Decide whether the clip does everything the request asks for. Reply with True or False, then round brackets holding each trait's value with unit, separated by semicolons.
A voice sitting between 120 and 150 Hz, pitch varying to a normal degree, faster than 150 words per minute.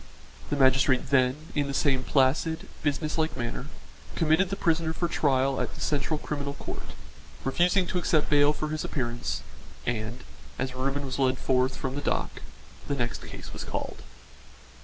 True (140 Hz; 3.1 semitones; 165 wpm)